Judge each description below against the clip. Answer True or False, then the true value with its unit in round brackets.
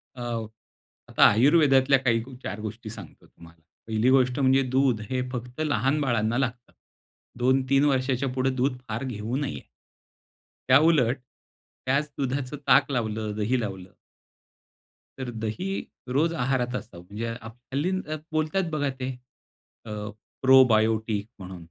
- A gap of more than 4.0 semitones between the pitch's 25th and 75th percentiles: False (3.5 semitones)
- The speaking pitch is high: False (125 Hz)